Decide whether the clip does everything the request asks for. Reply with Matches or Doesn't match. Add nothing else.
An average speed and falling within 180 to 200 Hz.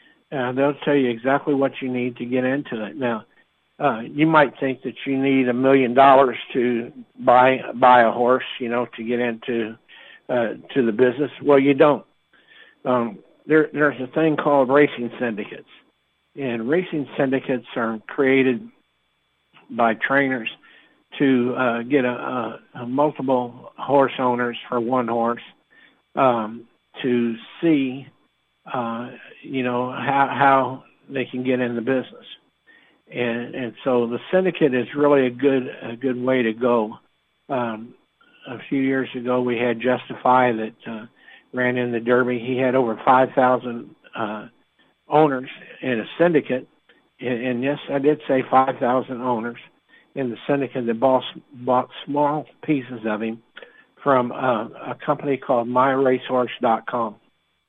Doesn't match